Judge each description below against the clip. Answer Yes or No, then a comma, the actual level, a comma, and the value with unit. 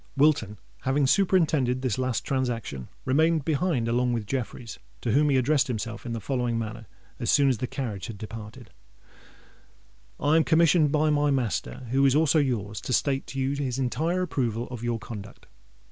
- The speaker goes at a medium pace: Yes, average, 175 wpm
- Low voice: Yes, low, 130 Hz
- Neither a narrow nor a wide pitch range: Yes, average, 3.9 semitones